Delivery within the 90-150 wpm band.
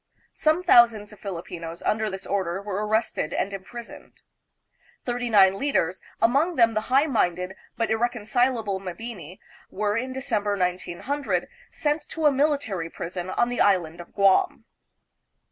Yes: average, 145 wpm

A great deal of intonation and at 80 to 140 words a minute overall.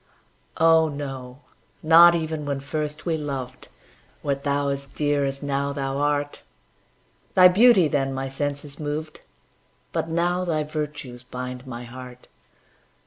No: narrow, 2.5 semitones; slow, 135 wpm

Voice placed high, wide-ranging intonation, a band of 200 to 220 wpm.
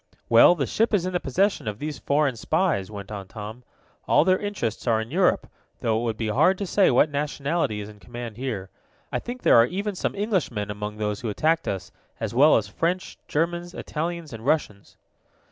No: low, 135 Hz; wide, 8.2 semitones; fast, 205 wpm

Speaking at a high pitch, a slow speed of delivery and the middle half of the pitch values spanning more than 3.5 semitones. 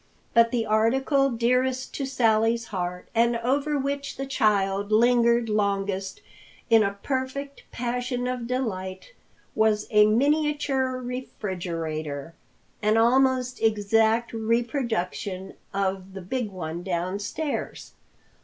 Yes: high, 230 Hz; slow, 105 wpm; average, 4.4 semitones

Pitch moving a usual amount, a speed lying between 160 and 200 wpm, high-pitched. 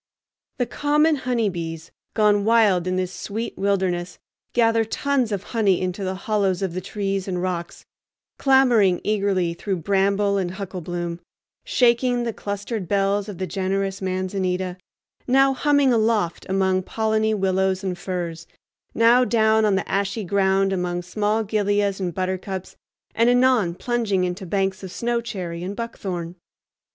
No: average, 3.1 semitones; average, 145 wpm; high, 195 Hz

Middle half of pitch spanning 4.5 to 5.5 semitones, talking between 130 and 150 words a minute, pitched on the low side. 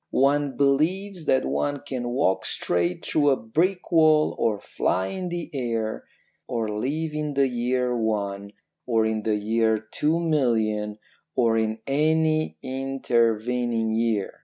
Yes: average, 5.0 semitones; slow, 135 wpm; low, 125 Hz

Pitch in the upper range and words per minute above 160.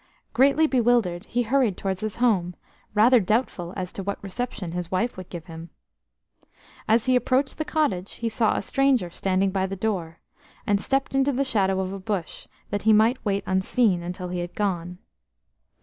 Yes: high, 200 Hz; average, 180 wpm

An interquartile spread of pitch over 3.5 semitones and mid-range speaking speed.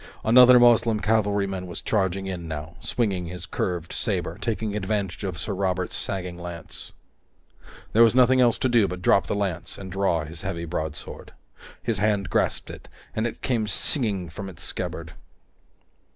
Yes: average, 3.9 semitones; average, 165 wpm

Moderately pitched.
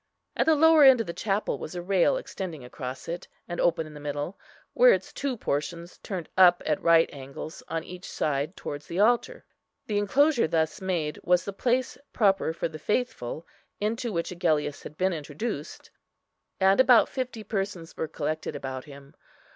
Yes: medium, 175 Hz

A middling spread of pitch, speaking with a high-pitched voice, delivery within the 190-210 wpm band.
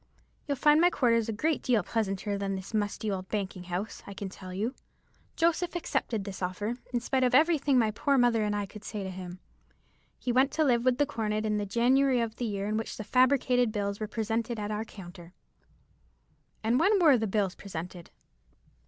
Yes: average, 4.1 semitones; high, 220 Hz; fast, 205 wpm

